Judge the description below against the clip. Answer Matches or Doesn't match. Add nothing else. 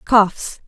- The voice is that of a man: Doesn't match